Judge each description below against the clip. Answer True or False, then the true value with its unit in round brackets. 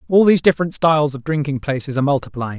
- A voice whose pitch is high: False (145 Hz)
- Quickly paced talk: True (210 wpm)